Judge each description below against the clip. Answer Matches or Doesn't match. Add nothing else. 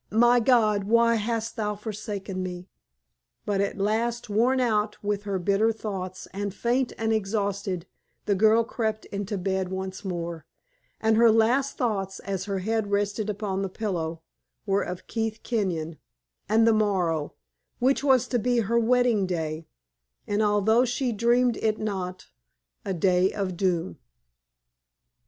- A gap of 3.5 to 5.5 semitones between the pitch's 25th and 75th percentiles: Doesn't match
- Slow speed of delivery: Doesn't match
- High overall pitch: Matches